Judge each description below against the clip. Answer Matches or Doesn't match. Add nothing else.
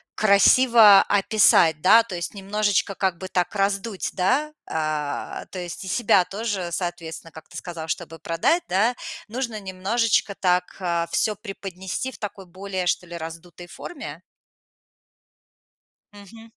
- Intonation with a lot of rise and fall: Doesn't match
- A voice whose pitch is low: Doesn't match